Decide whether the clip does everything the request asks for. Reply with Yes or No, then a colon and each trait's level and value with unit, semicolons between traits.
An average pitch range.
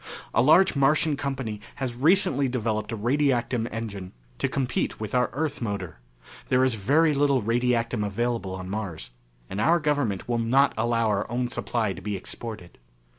Yes: average, 4.4 semitones